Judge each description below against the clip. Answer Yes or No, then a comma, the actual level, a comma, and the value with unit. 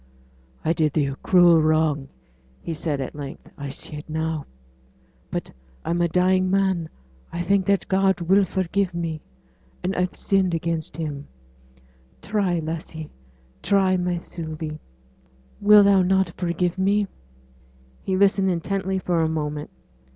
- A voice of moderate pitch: Yes, medium, 170 Hz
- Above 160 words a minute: No, average, 140 wpm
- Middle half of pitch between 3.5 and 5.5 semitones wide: No, average, 3.1 semitones